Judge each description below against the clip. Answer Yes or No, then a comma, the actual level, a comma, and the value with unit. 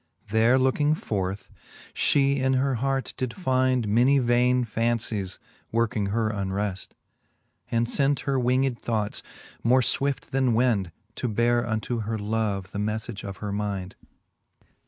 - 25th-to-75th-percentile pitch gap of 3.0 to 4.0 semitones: Yes, average, 3.7 semitones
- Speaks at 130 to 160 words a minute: Yes, slow, 135 wpm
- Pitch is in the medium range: No, low, 115 Hz